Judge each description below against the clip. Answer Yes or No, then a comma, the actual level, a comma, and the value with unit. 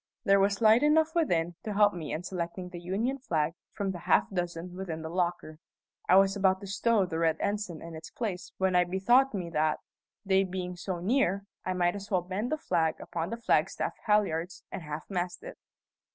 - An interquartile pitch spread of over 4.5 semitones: No, average, 3.0 semitones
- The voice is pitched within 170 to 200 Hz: Yes, medium, 185 Hz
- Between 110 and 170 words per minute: No, fast, 205 wpm